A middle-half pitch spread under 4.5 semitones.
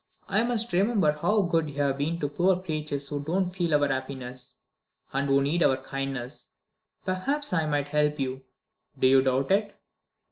No: average, 4.8 semitones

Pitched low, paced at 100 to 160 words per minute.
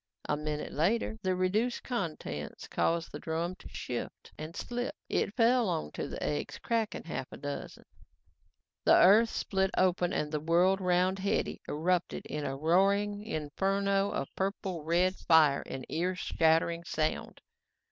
No: medium, 180 Hz; average, 145 wpm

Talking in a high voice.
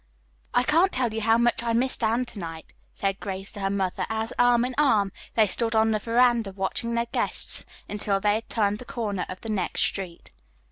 Yes: high, 220 Hz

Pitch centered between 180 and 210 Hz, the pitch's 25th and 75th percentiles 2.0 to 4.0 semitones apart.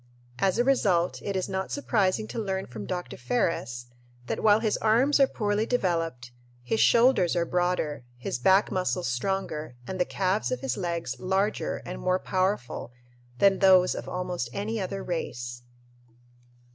Yes: medium, 185 Hz; average, 3.5 semitones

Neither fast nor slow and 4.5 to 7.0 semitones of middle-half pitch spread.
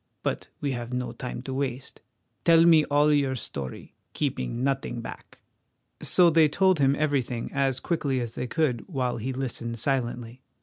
No: average, 165 wpm; average, 3.3 semitones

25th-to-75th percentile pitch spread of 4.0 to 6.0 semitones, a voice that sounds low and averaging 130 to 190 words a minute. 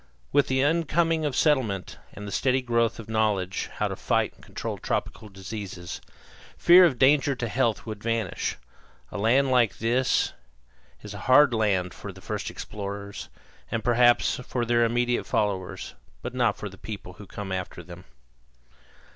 Yes: average, 4.3 semitones; low, 115 Hz; average, 165 wpm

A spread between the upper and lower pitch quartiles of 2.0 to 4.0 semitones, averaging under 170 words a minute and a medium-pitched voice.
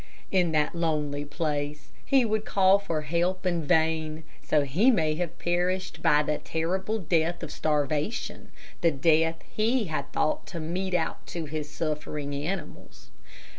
Yes: average, 3.3 semitones; average, 150 wpm; medium, 160 Hz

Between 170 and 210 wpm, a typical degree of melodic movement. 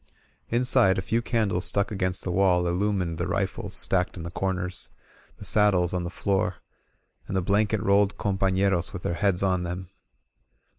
No: average, 175 wpm; narrow, 2.1 semitones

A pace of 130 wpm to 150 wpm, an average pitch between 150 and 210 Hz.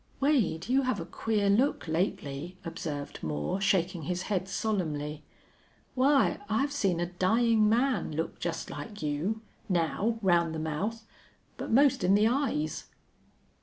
Yes: average, 140 wpm; high, 190 Hz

